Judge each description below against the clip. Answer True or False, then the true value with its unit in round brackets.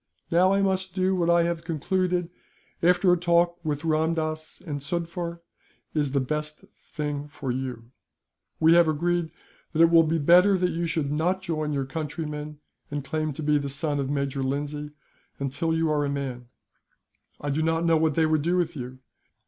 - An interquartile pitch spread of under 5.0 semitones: True (2.8 semitones)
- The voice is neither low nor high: True (155 Hz)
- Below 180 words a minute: False (185 wpm)